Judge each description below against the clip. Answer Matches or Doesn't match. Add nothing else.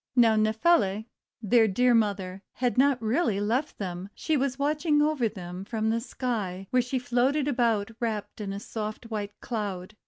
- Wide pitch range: Doesn't match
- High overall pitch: Matches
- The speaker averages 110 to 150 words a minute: Doesn't match